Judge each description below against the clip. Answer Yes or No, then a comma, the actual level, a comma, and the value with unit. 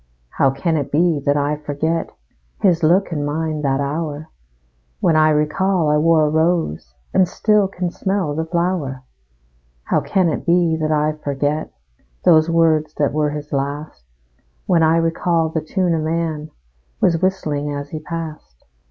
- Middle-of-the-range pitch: Yes, medium, 155 Hz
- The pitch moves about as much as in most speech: No, narrow, 2.2 semitones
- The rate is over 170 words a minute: No, average, 160 wpm